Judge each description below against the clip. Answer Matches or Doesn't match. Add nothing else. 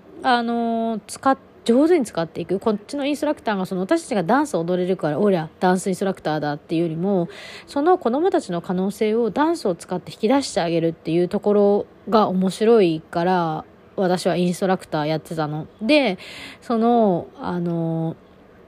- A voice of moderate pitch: Doesn't match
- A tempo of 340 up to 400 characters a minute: Matches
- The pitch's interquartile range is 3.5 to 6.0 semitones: Matches